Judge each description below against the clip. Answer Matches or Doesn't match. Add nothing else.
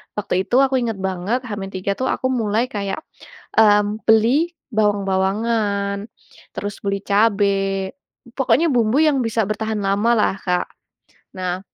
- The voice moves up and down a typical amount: Matches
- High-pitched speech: Matches